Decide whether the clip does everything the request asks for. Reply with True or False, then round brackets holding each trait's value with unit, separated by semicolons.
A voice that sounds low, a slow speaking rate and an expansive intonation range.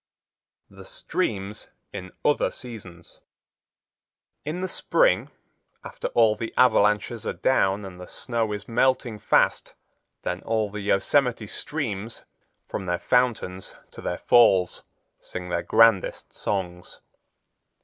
False (105 Hz; 120 wpm; 4.2 semitones)